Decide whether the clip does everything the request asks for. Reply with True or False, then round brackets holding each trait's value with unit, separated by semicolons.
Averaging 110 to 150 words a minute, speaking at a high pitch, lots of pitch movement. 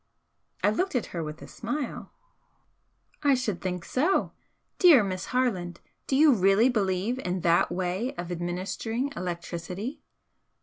True (135 wpm; 200 Hz; 6.2 semitones)